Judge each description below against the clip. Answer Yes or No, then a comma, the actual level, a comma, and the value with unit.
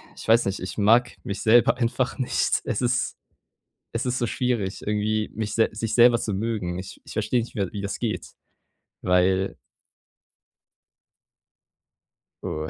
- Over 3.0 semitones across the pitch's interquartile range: Yes, average, 3.4 semitones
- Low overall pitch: Yes, low, 110 Hz